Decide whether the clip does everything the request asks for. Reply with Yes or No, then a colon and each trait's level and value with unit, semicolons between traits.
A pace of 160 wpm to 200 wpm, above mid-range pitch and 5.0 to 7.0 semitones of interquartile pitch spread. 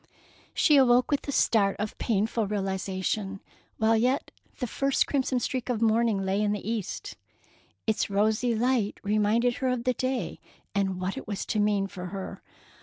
No: average, 170 wpm; high, 220 Hz; average, 3.7 semitones